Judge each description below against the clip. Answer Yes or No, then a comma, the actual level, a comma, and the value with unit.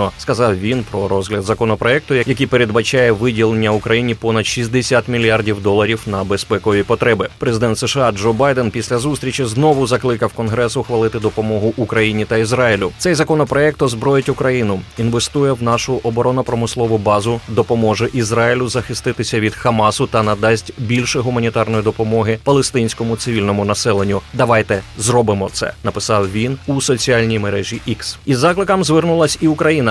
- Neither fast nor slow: Yes, average, 135 wpm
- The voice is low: Yes, low, 115 Hz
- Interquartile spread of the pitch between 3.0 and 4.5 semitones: No, narrow, 2.6 semitones